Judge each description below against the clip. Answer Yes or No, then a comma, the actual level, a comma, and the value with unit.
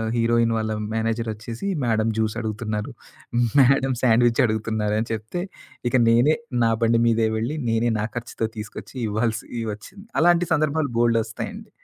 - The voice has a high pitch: No, low, 115 Hz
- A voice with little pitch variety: Yes, narrow, 1.7 semitones